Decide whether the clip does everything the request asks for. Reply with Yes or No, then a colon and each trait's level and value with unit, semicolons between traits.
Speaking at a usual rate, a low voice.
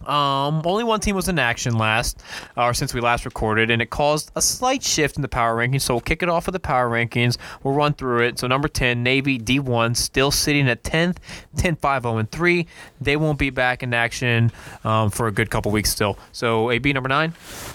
No: fast, 215 wpm; low, 130 Hz